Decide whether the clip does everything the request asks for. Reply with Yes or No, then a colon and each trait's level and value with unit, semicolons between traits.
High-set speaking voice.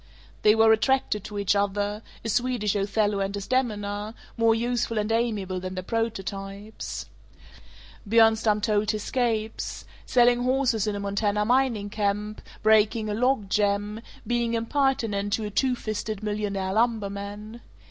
Yes: high, 215 Hz